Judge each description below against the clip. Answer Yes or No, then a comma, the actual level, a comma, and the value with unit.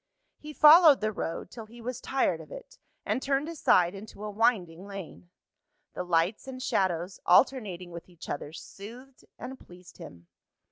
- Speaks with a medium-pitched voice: No, high, 210 Hz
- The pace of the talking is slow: No, average, 160 wpm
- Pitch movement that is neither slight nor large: No, wide, 7.0 semitones